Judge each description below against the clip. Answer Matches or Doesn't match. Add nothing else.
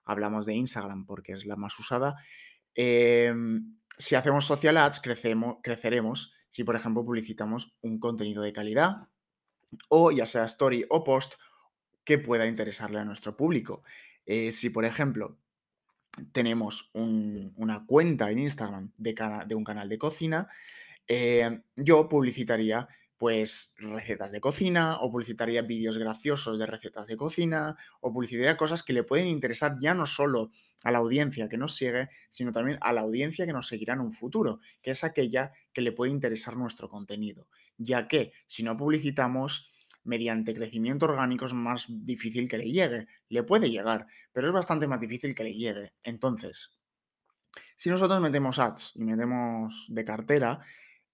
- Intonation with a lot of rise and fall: Doesn't match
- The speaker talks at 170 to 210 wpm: Doesn't match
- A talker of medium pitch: Doesn't match